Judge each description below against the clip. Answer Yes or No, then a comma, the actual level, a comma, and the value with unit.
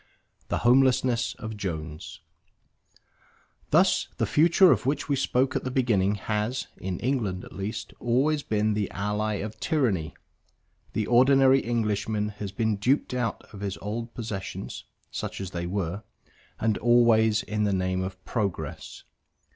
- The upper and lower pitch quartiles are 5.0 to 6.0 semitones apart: No, average, 3.7 semitones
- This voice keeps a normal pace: Yes, average, 145 wpm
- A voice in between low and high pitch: No, low, 110 Hz